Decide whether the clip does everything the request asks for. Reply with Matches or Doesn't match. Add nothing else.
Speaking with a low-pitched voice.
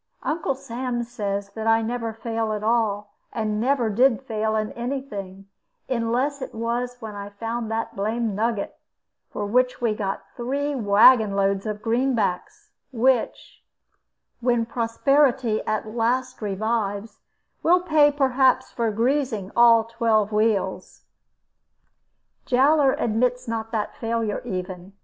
Doesn't match